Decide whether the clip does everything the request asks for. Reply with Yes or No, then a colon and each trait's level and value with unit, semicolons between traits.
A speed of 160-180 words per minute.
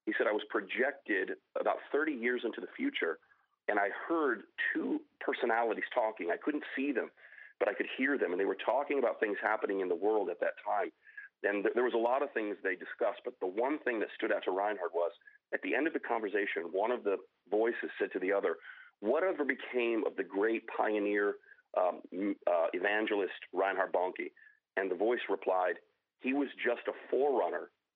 No: average, 200 wpm